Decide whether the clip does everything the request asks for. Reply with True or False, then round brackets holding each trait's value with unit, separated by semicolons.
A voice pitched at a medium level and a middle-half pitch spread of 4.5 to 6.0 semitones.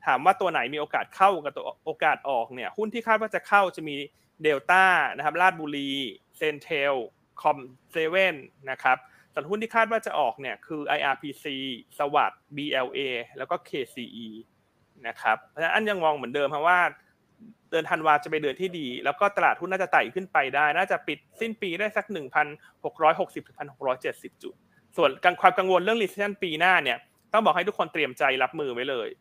True (160 Hz; 5.4 semitones)